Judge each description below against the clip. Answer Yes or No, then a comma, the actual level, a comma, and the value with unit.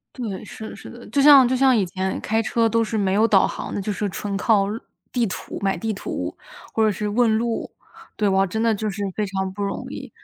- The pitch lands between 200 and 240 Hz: Yes, high, 215 Hz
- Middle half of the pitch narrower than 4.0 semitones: Yes, average, 2.7 semitones